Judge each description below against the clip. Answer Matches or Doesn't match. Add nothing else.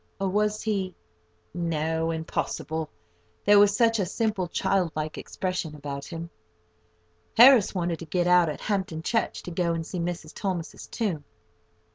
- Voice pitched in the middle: Matches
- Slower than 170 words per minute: Matches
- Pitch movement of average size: Matches